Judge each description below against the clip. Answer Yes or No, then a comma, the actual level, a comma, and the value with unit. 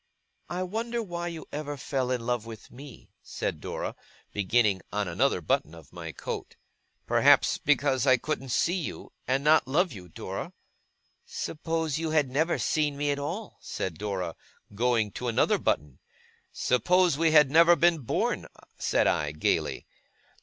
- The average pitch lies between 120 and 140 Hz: Yes, low, 135 Hz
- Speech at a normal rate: Yes, average, 155 wpm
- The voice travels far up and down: Yes, wide, 6.9 semitones